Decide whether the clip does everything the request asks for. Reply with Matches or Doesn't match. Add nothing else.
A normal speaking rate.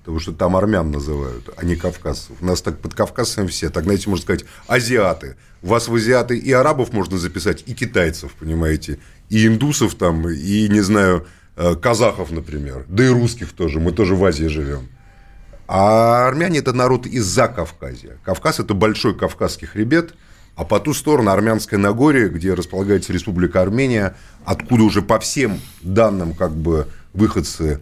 Doesn't match